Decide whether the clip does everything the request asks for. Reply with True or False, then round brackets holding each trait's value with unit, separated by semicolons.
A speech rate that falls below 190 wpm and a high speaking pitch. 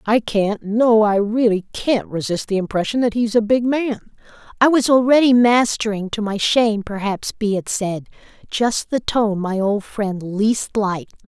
True (165 wpm; 215 Hz)